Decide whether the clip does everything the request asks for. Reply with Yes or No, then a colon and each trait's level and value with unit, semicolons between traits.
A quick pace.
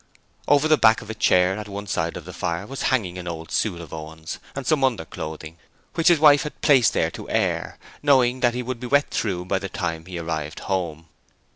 Yes: fast, 225 wpm